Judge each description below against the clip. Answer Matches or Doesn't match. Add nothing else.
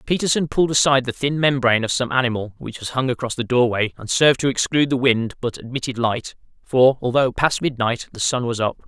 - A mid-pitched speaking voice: Doesn't match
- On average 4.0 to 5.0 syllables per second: Doesn't match